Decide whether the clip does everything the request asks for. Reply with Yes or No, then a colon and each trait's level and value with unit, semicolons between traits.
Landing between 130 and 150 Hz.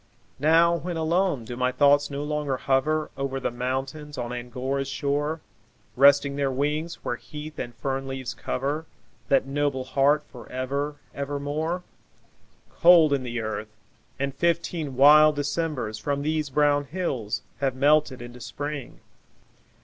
Yes: medium, 140 Hz